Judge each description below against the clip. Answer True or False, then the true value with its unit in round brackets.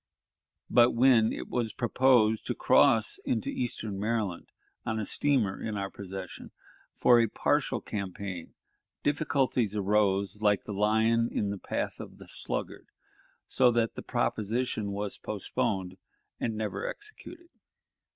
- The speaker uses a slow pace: True (130 wpm)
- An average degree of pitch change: True (3.0 semitones)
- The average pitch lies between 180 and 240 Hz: False (110 Hz)